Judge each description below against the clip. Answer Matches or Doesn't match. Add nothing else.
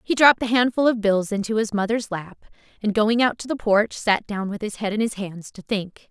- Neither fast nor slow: Doesn't match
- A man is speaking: Doesn't match